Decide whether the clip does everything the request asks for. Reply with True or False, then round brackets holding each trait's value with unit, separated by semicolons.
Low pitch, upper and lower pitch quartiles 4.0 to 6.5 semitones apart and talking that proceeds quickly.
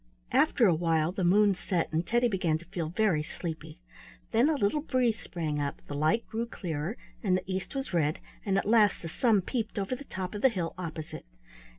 False (185 Hz; 5.3 semitones; 210 wpm)